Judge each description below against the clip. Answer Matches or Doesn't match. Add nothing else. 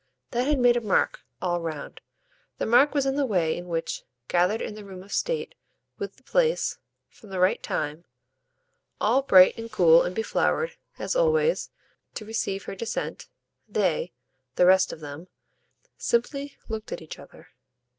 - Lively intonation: Matches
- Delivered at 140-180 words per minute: Matches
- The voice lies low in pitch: Doesn't match